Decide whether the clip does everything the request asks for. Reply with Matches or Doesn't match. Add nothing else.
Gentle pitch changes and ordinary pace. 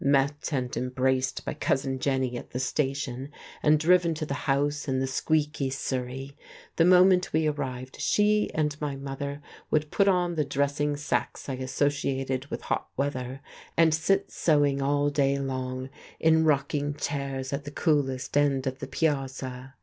Matches